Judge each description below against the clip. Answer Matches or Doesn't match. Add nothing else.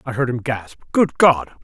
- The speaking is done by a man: Matches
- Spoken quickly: Matches